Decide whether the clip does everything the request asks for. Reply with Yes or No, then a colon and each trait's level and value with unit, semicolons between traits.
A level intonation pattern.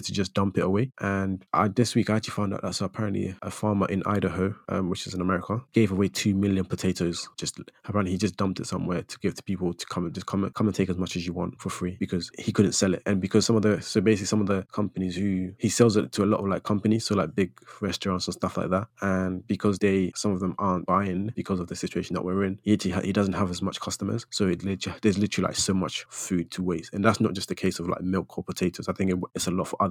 Yes: narrow, 2.1 semitones